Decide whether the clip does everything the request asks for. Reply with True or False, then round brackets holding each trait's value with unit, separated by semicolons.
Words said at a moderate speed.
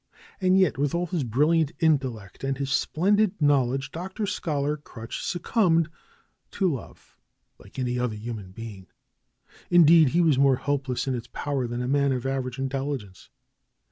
True (155 wpm)